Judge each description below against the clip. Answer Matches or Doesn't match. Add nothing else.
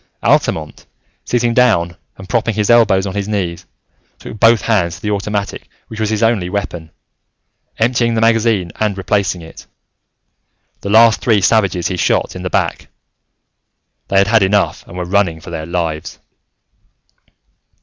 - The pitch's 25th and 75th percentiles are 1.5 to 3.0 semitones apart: Doesn't match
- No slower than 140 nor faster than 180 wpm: Matches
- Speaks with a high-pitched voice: Doesn't match